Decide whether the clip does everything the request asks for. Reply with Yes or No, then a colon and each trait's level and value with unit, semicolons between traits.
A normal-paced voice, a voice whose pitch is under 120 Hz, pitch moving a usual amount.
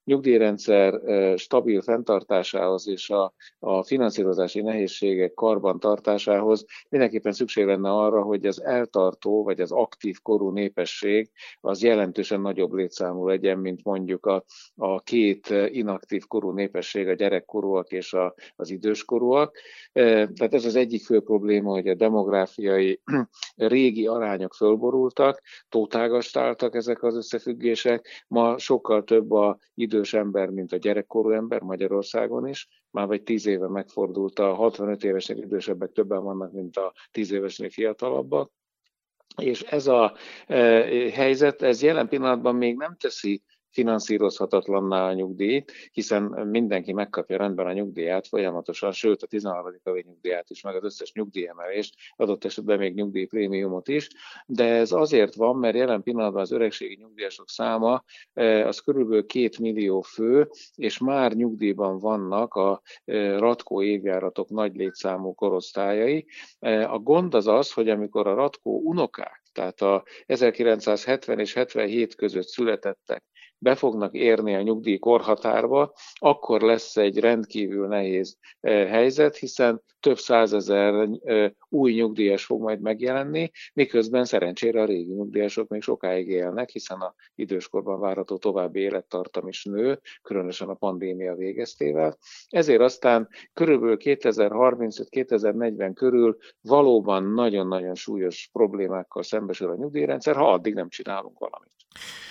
Yes: average, 125 wpm; low, 105 Hz; average, 3.2 semitones